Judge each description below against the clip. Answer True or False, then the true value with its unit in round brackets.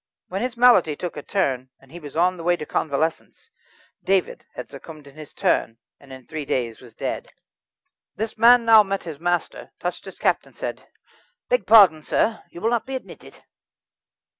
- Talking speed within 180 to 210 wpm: True (190 wpm)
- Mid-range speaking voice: True (175 Hz)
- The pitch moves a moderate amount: False (6.9 semitones)